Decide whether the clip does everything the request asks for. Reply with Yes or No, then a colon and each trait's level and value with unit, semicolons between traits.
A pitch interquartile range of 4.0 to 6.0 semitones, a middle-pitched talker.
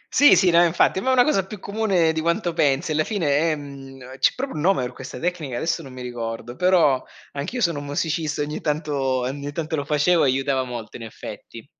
Yes: average, 4.5 semitones; medium, 150 Hz